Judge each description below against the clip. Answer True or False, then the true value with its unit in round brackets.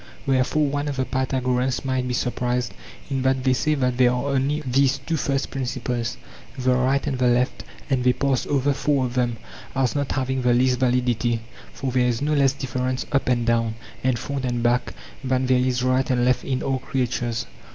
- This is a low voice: True (130 Hz)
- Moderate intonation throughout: False (1.4 semitones)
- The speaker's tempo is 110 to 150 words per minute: False (205 wpm)